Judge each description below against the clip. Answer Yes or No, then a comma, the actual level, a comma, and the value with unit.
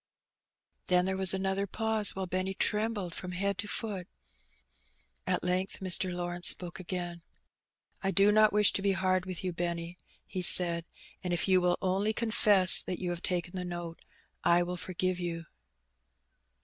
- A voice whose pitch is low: No, medium, 185 Hz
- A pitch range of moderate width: No, narrow, 1.7 semitones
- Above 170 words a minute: No, average, 165 wpm